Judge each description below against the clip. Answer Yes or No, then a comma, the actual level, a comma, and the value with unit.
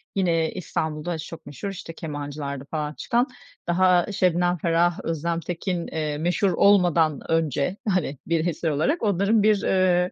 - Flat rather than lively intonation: No, average, 3.0 semitones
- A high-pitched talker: No, medium, 170 Hz